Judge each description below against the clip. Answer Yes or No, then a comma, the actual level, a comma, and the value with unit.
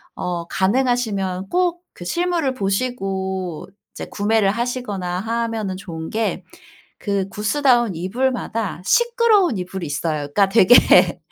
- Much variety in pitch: No, average, 4.8 semitones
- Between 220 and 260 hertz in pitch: No, high, 205 Hz